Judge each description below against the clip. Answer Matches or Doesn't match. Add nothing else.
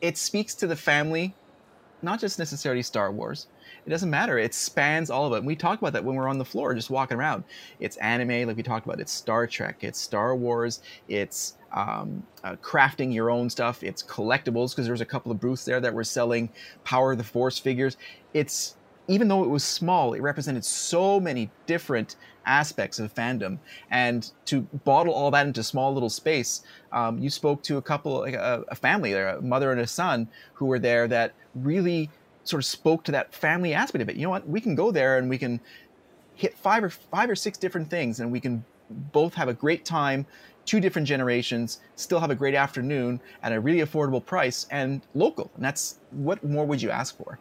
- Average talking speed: Doesn't match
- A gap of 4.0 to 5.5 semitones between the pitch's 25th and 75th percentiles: Matches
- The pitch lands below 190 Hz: Matches